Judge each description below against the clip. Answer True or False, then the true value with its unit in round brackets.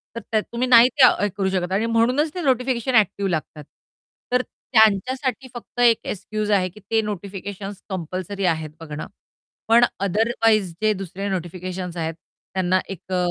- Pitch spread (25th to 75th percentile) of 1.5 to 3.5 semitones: False (4.0 semitones)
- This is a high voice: True (205 Hz)